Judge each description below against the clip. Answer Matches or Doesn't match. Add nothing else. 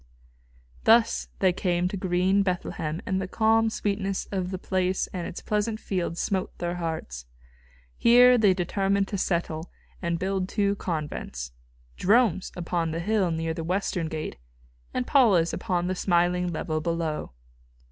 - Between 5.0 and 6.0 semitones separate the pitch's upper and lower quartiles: Doesn't match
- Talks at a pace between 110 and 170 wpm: Matches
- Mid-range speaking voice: Matches